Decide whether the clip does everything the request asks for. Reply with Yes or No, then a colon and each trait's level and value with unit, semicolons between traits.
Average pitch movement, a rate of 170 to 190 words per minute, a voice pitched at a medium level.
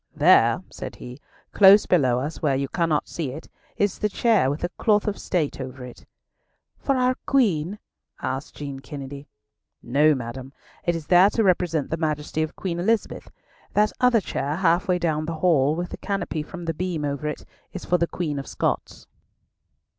Yes: average, 4.6 semitones; average, 185 wpm; medium, 160 Hz